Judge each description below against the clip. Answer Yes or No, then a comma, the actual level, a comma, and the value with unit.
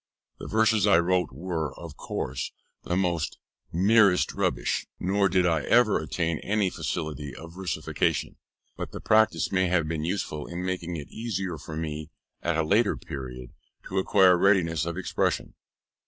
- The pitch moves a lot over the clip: No, average, 3.4 semitones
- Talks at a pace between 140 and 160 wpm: Yes, average, 155 wpm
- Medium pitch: No, very low, 90 Hz